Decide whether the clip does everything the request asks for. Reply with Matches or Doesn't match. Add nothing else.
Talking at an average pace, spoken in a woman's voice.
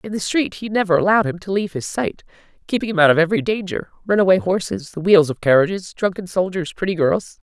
Doesn't match